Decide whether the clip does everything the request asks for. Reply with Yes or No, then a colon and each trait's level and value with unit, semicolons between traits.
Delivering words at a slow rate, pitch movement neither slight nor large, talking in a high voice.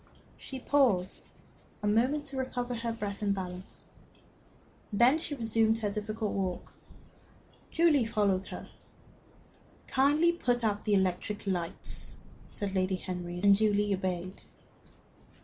Yes: slow, 115 wpm; average, 4.4 semitones; high, 210 Hz